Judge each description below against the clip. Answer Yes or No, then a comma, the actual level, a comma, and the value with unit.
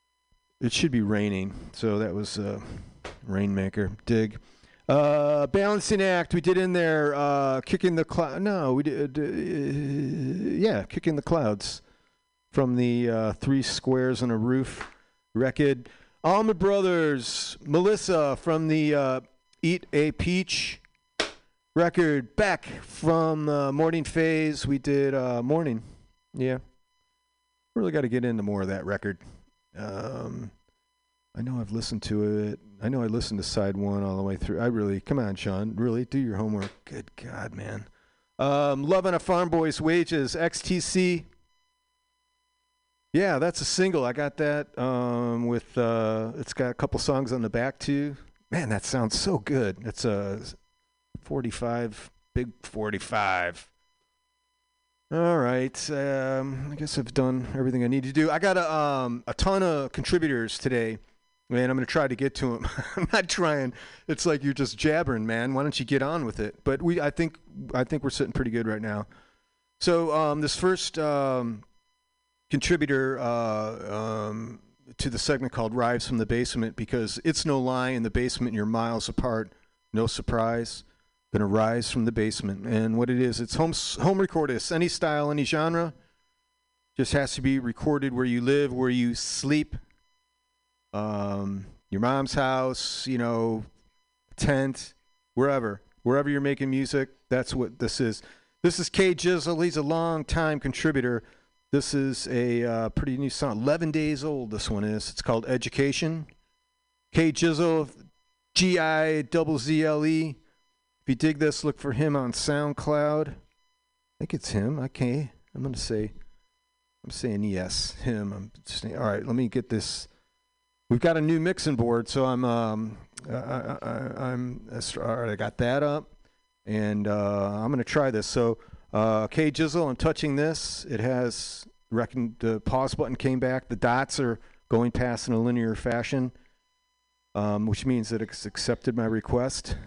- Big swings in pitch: Yes, wide, 5.8 semitones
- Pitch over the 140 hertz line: No, low, 135 Hz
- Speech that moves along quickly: No, average, 165 wpm